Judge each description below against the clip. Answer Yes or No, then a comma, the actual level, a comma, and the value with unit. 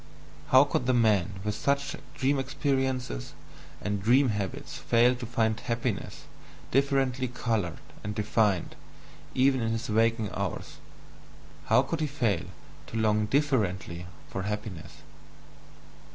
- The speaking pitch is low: Yes, low, 115 Hz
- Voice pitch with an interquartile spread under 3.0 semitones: No, average, 4.0 semitones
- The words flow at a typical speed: No, slow, 125 wpm